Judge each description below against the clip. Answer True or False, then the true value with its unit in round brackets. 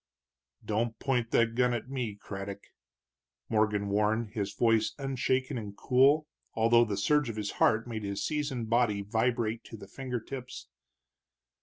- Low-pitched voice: True (115 Hz)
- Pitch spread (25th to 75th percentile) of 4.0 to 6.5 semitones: False (3.0 semitones)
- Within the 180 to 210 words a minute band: False (150 wpm)